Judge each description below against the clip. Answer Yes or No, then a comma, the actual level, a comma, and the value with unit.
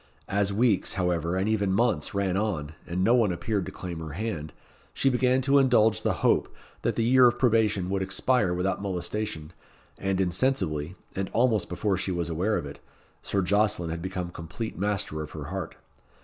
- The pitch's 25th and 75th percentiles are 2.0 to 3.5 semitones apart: No, average, 3.9 semitones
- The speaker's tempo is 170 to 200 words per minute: Yes, average, 185 wpm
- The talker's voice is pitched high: No, very low, 95 Hz